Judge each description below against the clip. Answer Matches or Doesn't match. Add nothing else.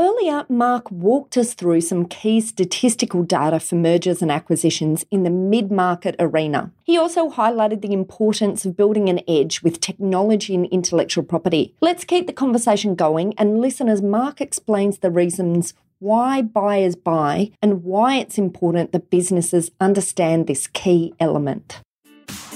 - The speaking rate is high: Doesn't match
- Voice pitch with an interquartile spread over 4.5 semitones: Doesn't match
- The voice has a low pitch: Doesn't match